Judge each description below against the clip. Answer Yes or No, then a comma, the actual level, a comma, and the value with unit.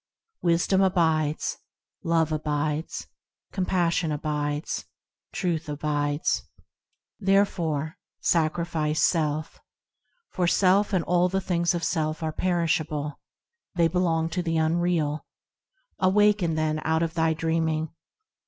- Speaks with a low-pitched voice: No, medium, 165 Hz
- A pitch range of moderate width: No, narrow, 2.2 semitones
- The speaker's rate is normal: No, slow, 105 wpm